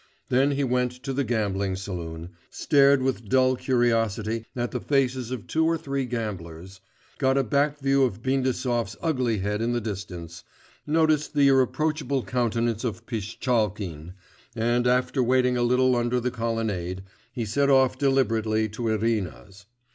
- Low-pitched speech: Yes, low, 120 Hz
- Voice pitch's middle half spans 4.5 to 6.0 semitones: No, average, 3.7 semitones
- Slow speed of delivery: No, average, 150 wpm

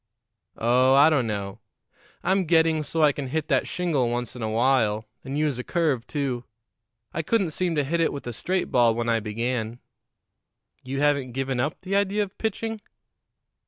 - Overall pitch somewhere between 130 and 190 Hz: Yes, medium, 140 Hz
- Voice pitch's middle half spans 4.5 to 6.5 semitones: Yes, average, 5.1 semitones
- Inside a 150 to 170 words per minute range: No, average, 185 wpm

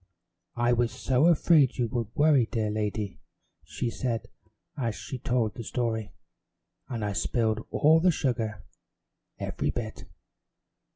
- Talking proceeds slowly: Yes, slow, 130 wpm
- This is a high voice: No, low, 120 Hz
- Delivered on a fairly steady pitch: No, average, 3.0 semitones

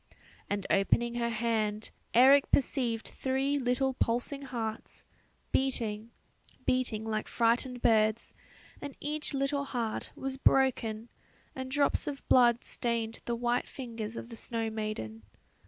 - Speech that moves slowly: Yes, slow, 125 wpm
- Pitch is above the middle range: Yes, high, 235 Hz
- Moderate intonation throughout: Yes, average, 3.1 semitones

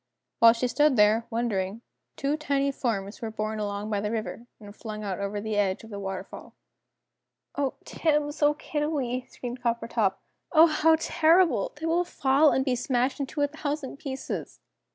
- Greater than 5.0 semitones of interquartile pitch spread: Yes, wide, 5.6 semitones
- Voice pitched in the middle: No, high, 245 Hz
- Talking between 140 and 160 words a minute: No, average, 170 wpm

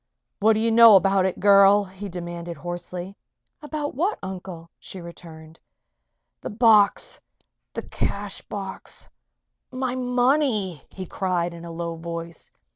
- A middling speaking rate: No, slow, 130 wpm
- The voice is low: No, high, 190 Hz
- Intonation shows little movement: No, average, 4.4 semitones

